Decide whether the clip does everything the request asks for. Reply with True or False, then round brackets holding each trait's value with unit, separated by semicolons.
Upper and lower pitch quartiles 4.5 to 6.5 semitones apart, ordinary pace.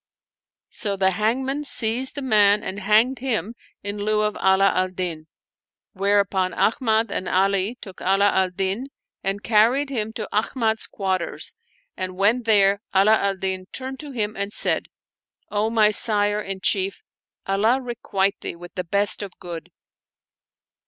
False (2.6 semitones; 150 wpm)